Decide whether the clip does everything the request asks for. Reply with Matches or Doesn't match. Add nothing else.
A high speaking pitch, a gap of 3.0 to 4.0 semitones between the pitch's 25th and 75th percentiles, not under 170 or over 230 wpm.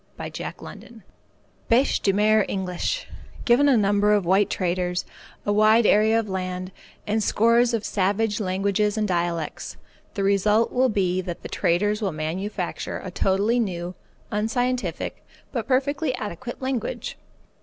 Doesn't match